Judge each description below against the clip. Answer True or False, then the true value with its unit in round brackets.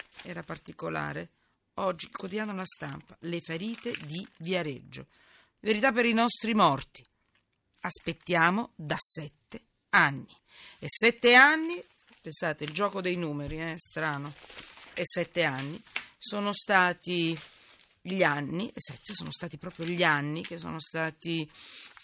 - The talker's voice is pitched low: False (175 Hz)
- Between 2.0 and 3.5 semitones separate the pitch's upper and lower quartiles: False (4.6 semitones)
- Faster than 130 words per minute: False (125 wpm)